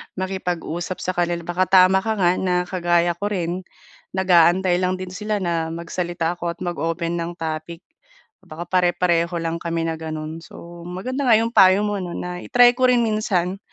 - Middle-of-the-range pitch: Yes, medium, 180 Hz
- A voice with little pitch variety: Yes, narrow, 1.8 semitones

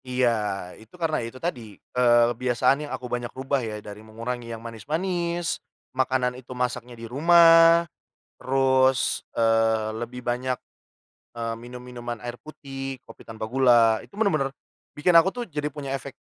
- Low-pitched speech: Yes, low, 125 Hz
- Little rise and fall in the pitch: No, average, 3.5 semitones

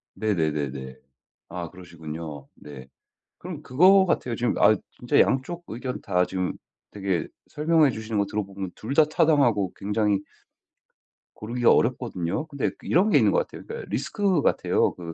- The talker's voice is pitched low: Yes, low, 110 Hz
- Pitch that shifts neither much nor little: No, wide, 8.8 semitones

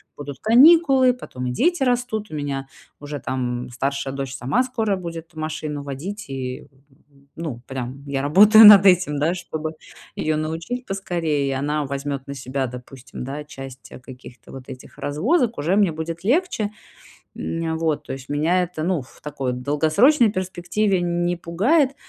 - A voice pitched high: No, medium, 155 Hz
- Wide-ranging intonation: Yes, wide, 6.4 semitones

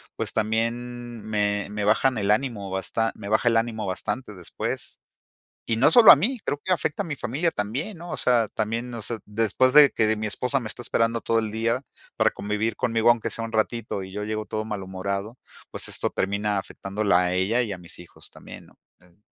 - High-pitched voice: No, low, 110 Hz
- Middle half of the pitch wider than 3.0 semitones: No, average, 2.7 semitones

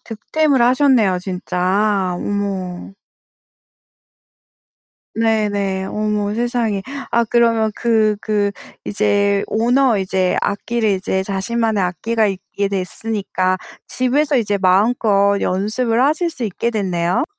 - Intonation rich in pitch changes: No, average, 3.3 semitones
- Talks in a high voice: Yes, high, 210 Hz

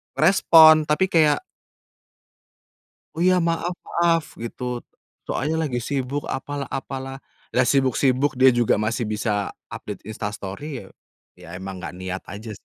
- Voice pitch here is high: No, low, 130 Hz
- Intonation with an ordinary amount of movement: No, wide, 6.0 semitones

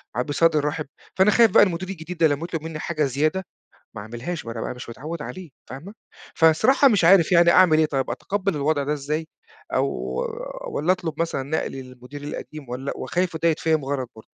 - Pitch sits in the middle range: Yes, medium, 155 Hz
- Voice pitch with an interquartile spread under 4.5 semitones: Yes, average, 3.7 semitones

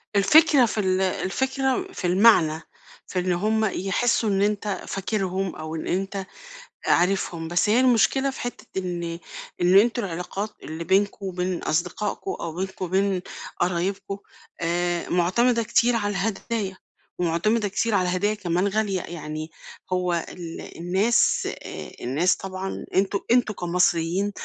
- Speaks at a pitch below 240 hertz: Yes, high, 190 Hz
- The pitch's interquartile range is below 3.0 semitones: No, average, 3.3 semitones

